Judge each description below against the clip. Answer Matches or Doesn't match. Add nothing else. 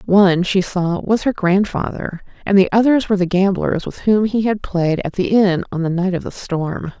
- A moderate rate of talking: Doesn't match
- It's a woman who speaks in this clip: Matches